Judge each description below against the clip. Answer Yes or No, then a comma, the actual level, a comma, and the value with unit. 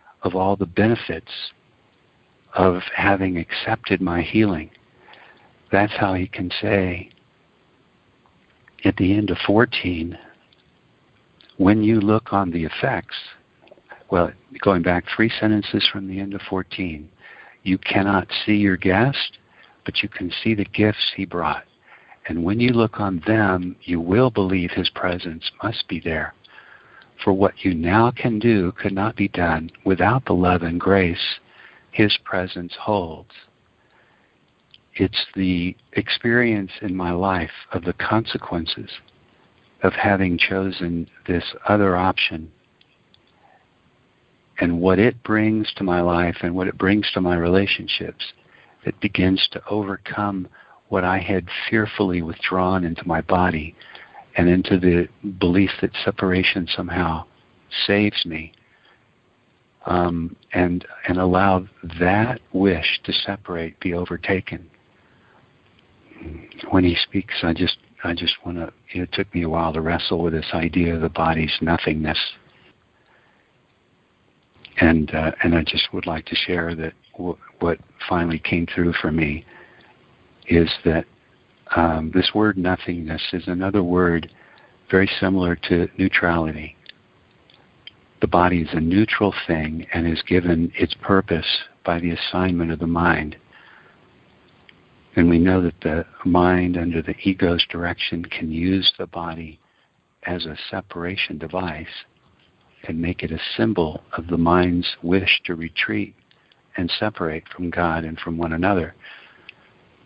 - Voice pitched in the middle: No, very low, 90 Hz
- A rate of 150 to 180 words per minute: No, slow, 135 wpm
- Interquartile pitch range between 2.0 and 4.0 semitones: Yes, narrow, 2.6 semitones